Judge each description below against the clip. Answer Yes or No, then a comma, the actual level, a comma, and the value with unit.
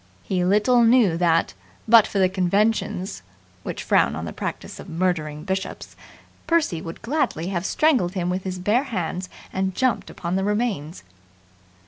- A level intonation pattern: No, average, 3.8 semitones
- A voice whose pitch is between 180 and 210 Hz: Yes, high, 190 Hz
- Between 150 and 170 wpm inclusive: Yes, average, 155 wpm